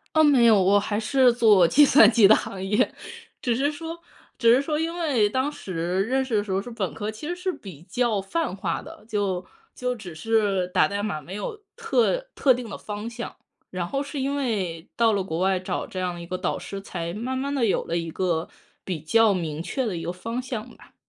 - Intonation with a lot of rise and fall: Yes, wide, 5.8 semitones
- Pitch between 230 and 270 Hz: No, high, 215 Hz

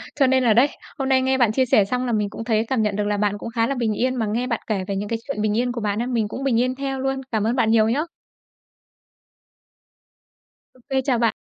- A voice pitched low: No, high, 235 Hz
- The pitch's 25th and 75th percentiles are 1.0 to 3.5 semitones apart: Yes, average, 3.2 semitones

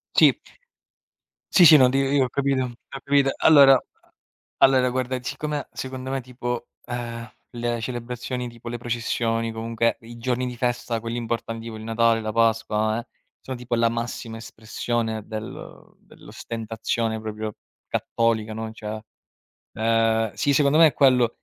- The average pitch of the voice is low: Yes, low, 120 Hz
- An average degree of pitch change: No, narrow, 2.1 semitones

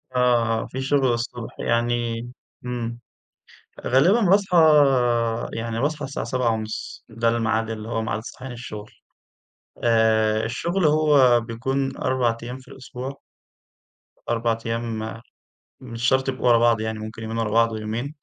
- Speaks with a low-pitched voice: Yes, low, 115 Hz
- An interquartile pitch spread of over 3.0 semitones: No, narrow, 2.5 semitones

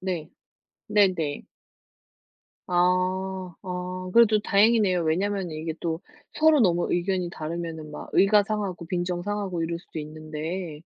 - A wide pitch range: No, average, 3.0 semitones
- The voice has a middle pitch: Yes, medium, 180 Hz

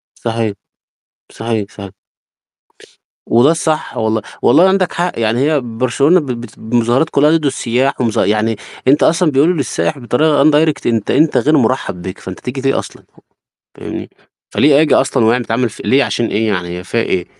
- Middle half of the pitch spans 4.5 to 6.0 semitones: Yes, average, 5.0 semitones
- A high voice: No, low, 125 Hz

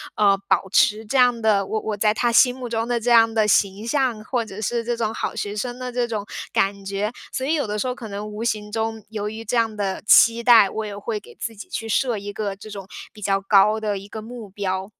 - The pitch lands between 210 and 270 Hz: Yes, high, 215 Hz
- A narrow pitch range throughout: Yes, narrow, 2.3 semitones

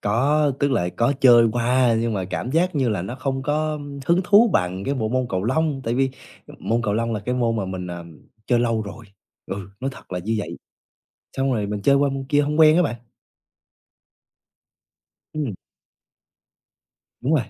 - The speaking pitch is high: No, low, 125 Hz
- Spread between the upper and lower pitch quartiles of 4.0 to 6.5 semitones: Yes, average, 5.0 semitones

